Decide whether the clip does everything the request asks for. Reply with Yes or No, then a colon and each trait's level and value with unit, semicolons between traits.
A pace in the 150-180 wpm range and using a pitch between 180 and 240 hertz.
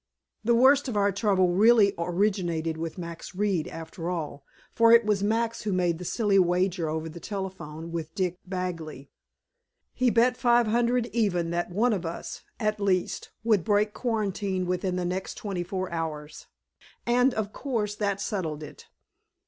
Yes: average, 165 wpm; high, 190 Hz